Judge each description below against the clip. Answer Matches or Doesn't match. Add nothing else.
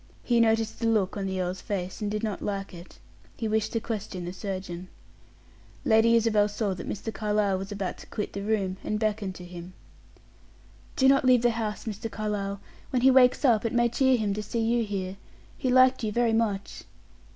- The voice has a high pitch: Matches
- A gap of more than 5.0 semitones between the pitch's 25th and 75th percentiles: Doesn't match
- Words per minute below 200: Doesn't match